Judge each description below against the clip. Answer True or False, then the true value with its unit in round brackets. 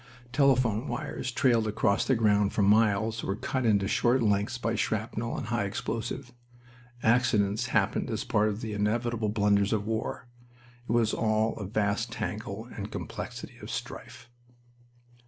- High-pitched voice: False (110 Hz)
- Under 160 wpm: True (150 wpm)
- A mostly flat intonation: True (2.2 semitones)